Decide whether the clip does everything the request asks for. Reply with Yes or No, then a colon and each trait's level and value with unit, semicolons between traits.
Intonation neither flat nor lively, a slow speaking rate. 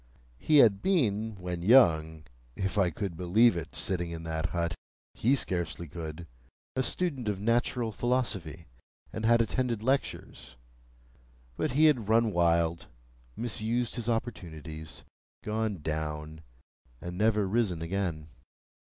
No: wide, 5.8 semitones; slow, 125 wpm